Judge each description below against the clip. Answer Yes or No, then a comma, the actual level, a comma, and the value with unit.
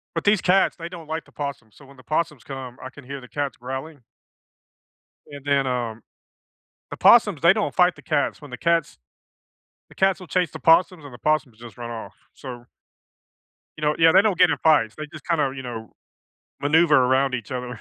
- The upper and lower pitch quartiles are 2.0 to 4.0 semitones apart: No, average, 4.7 semitones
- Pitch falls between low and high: Yes, medium, 145 Hz